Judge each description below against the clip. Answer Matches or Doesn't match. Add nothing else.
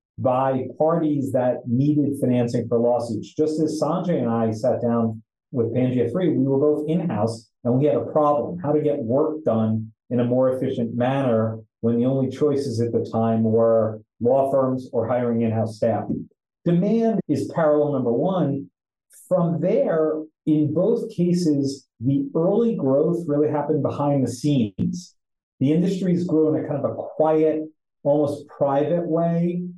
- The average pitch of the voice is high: Doesn't match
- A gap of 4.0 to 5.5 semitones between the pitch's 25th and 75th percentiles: Matches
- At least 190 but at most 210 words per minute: Doesn't match